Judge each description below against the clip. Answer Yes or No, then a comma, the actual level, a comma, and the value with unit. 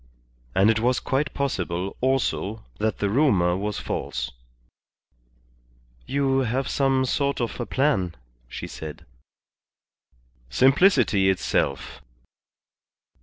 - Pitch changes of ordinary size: No, wide, 5.9 semitones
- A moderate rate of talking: No, slow, 100 wpm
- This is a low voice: Yes, low, 115 Hz